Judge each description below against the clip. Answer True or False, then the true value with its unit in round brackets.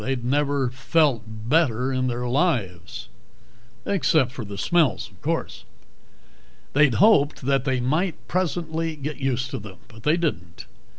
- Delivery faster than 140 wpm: False (135 wpm)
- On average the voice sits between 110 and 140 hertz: True (135 Hz)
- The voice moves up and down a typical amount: True (4.6 semitones)